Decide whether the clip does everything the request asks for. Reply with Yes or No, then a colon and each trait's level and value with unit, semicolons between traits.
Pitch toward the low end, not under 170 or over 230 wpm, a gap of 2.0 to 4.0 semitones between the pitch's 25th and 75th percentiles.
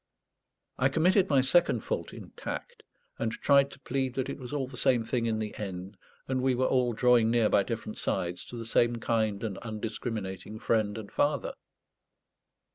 Yes: low, 120 Hz; average, 185 wpm; average, 3.2 semitones